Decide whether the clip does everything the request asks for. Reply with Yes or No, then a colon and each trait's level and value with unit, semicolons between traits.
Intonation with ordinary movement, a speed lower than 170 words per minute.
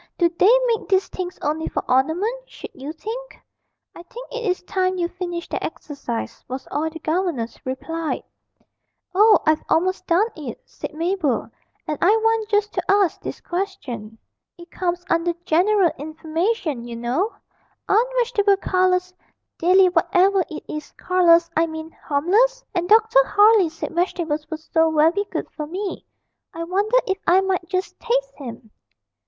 Yes: average, 4.1 semitones; average, 160 wpm